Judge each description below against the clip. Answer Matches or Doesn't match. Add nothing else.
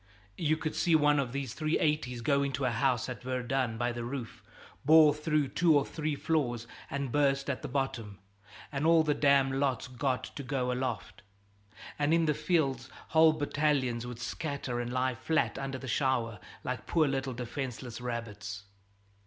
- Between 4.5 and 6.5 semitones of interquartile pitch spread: Doesn't match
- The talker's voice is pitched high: Doesn't match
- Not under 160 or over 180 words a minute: Matches